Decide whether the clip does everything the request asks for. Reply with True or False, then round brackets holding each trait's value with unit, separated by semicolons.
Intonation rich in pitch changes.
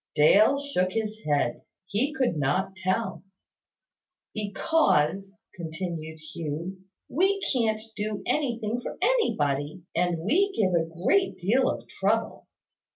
True (6.3 semitones)